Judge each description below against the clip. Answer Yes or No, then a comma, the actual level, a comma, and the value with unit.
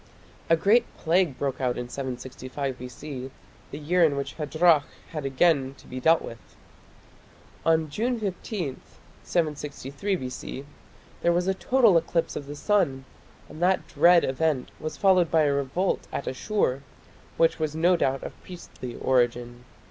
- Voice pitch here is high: No, medium, 150 Hz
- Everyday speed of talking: Yes, average, 150 wpm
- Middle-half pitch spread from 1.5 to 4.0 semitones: No, average, 4.9 semitones